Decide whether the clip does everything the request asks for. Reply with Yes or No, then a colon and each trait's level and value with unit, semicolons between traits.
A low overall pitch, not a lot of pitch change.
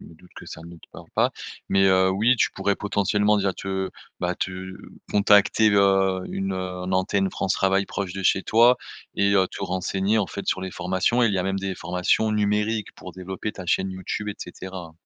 Yes: very low, 95 Hz; narrow, 1.6 semitones